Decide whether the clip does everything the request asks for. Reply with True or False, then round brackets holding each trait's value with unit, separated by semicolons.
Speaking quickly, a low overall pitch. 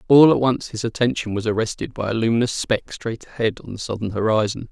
True (215 wpm; 115 Hz)